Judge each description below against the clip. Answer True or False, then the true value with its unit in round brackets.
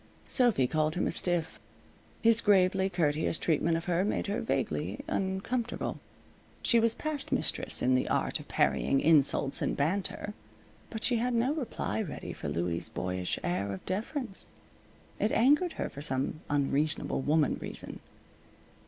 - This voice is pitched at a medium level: True (180 Hz)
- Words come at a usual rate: True (150 wpm)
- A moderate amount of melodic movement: False (7.8 semitones)